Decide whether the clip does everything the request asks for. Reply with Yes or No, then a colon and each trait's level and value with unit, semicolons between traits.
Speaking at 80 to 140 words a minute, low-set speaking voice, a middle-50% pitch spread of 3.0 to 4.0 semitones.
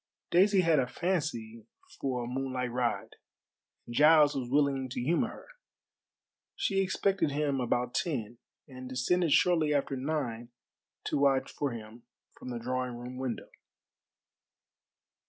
Yes: slow, 135 wpm; low, 130 Hz; average, 3.6 semitones